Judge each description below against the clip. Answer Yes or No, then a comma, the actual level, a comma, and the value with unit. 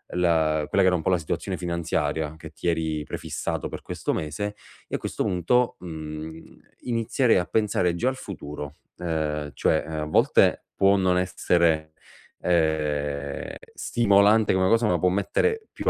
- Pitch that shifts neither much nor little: Yes, average, 4.0 semitones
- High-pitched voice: No, very low, 85 Hz